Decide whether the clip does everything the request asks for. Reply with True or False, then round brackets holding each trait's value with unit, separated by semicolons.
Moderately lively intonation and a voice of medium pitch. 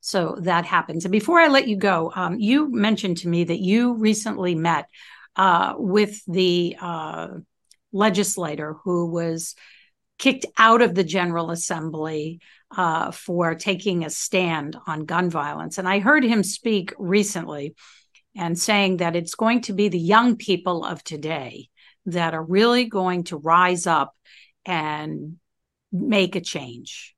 True (3.7 semitones; 180 Hz)